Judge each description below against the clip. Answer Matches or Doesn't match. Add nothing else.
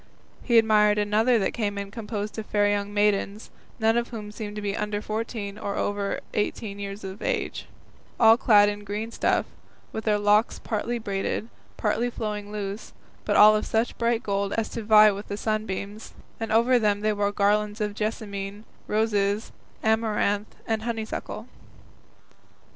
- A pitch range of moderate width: Doesn't match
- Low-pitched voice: Doesn't match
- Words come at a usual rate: Matches